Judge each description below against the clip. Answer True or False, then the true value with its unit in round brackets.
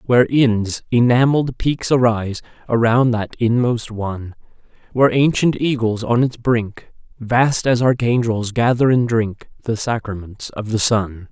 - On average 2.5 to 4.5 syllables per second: True (4.4 syllables/s)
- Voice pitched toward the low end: True (115 Hz)